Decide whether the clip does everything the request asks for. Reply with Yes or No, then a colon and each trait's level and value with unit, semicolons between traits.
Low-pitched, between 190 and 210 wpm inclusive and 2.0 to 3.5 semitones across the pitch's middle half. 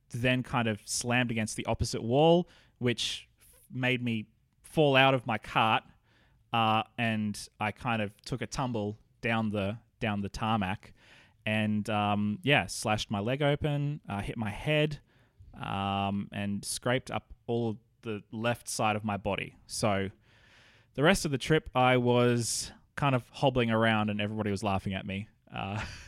No: low, 115 Hz; average, 165 wpm; average, 3.2 semitones